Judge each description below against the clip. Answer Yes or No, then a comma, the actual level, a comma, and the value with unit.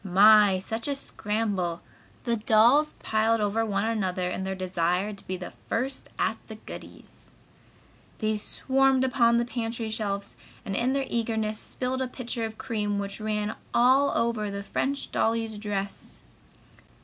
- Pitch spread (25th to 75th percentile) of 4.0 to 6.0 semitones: No, average, 2.8 semitones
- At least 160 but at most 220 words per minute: No, average, 150 wpm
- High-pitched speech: Yes, high, 220 Hz